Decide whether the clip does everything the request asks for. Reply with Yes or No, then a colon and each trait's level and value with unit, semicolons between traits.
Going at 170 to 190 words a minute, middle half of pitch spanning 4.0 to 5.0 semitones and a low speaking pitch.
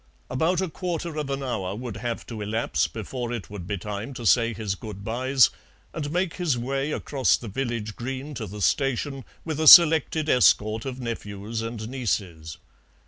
Yes: average, 180 wpm; average, 4.4 semitones; low, 120 Hz